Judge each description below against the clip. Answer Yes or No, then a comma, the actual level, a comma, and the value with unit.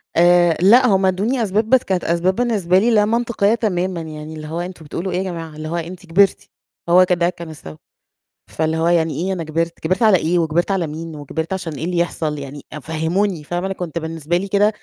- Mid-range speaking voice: Yes, medium, 175 Hz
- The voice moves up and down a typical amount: Yes, average, 3.0 semitones